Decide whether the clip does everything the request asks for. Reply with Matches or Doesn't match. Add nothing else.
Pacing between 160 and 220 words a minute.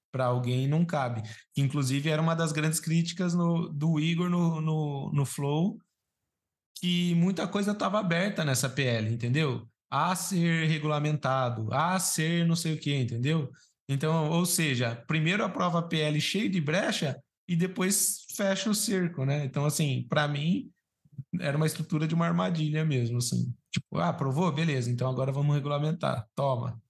Matches